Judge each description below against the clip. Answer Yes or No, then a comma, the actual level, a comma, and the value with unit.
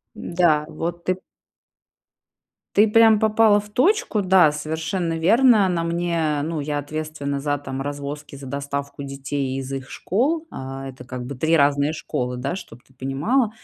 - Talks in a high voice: No, medium, 150 Hz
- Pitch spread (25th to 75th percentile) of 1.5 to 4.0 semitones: No, average, 4.8 semitones